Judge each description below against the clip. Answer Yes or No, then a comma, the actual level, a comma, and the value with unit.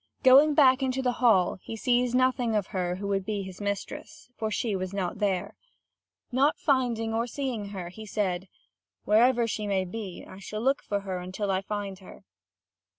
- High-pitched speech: Yes, high, 210 Hz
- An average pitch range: Yes, average, 4.3 semitones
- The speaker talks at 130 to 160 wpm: No, average, 185 wpm